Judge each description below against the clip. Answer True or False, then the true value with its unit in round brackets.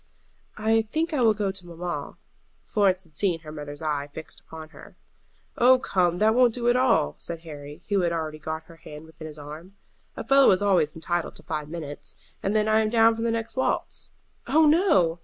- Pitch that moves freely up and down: True (6.1 semitones)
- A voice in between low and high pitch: True (180 Hz)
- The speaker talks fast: True (210 wpm)